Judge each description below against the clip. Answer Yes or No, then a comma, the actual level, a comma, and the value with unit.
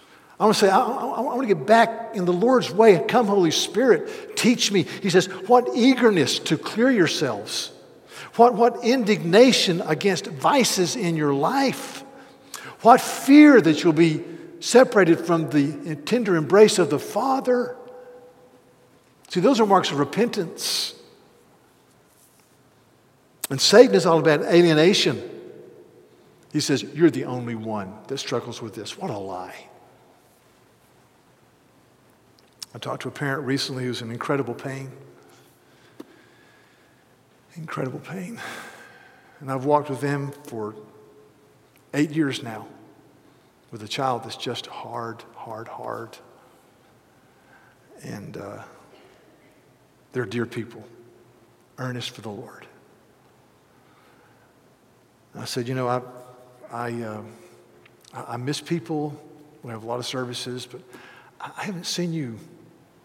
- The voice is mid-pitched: Yes, medium, 155 Hz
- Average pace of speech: No, slow, 125 wpm